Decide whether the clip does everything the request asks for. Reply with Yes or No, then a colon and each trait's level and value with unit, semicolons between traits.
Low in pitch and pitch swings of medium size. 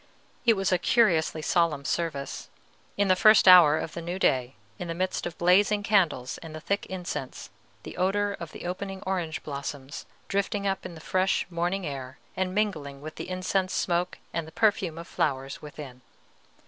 No: medium, 175 Hz; average, 3.9 semitones